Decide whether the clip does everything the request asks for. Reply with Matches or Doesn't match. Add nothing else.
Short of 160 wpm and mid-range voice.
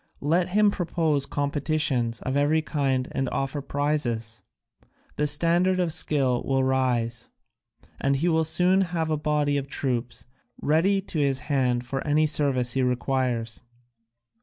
Matches